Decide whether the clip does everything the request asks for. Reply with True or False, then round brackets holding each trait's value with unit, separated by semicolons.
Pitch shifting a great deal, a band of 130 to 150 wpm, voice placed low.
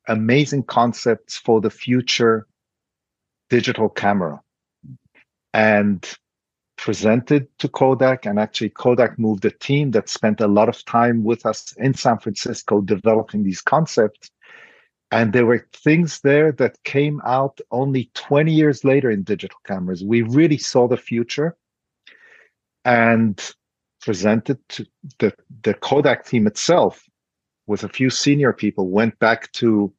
False (3.8 semitones; 135 wpm; 120 Hz)